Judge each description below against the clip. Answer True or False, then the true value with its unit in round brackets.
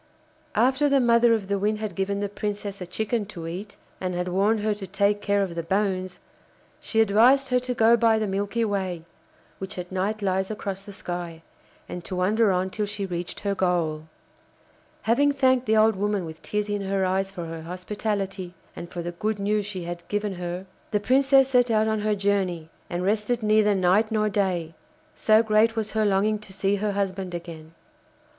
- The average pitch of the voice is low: False (200 Hz)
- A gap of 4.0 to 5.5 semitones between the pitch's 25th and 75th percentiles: False (2.8 semitones)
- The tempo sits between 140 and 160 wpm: False (200 wpm)